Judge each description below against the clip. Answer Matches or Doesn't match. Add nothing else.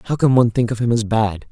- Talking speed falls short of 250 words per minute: Doesn't match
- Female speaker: Doesn't match